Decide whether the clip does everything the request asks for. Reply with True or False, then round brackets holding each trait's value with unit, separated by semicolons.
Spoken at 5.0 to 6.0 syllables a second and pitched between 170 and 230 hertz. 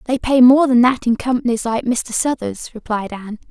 False (5.3 syllables/s; 240 Hz)